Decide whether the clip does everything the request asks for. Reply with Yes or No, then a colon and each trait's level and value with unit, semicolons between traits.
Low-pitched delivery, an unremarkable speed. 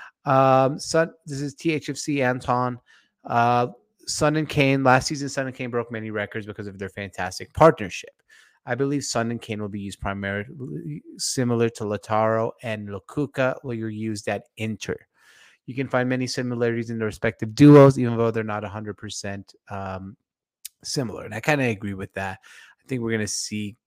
Yes: low, 115 Hz; average, 180 wpm